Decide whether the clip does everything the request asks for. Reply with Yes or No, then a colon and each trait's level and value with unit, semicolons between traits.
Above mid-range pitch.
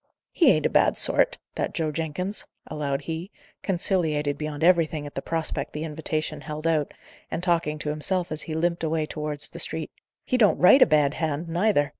No: medium, 155 Hz